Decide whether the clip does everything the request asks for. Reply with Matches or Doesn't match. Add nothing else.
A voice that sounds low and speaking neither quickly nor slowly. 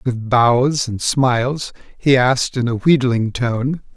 Matches